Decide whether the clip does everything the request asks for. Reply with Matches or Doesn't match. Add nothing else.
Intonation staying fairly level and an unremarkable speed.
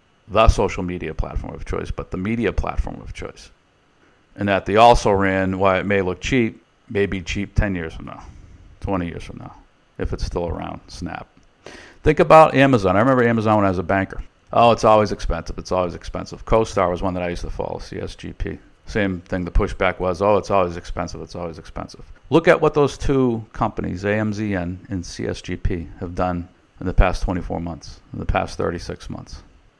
Doesn't match